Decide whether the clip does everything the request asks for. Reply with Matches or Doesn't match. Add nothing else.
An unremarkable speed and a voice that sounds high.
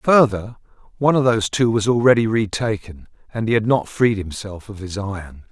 Doesn't match